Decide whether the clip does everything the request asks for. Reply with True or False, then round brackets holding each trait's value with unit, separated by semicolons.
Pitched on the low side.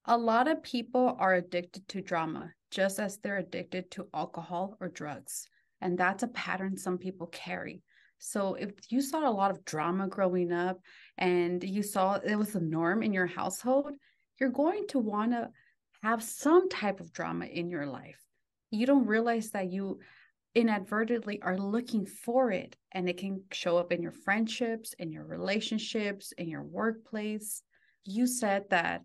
False (200 Hz)